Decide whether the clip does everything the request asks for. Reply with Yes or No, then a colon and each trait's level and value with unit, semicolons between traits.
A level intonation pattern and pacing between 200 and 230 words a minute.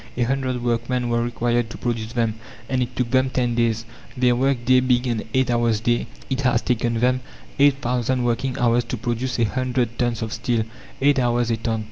Yes: narrow, 1.5 semitones; fast, 205 wpm